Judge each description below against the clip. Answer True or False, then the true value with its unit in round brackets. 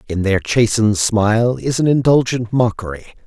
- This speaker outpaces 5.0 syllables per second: True (5.2 syllables/s)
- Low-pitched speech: True (115 Hz)